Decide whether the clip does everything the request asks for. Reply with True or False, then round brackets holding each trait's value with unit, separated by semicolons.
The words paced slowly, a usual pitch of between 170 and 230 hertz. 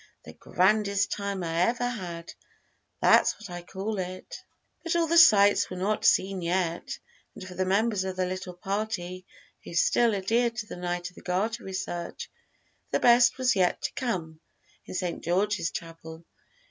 False (170 wpm; 190 Hz)